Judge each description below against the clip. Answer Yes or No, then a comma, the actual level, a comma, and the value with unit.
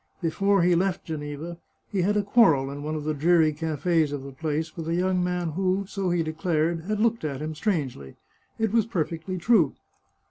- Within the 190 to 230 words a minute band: Yes, average, 200 wpm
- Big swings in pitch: No, average, 3.5 semitones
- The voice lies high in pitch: No, medium, 165 Hz